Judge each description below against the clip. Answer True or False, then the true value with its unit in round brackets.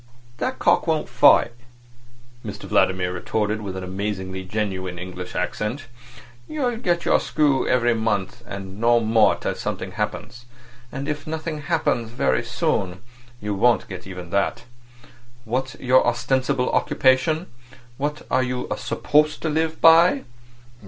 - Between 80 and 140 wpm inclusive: True (135 wpm)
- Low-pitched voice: True (120 Hz)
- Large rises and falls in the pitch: True (6.8 semitones)